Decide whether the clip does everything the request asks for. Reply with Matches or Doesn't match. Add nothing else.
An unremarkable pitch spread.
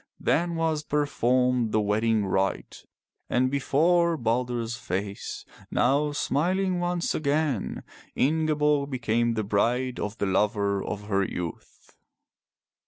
Doesn't match